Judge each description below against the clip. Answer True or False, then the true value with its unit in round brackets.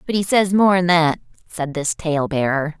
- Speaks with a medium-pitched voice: True (165 Hz)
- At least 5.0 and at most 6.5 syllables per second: False (4.7 syllables/s)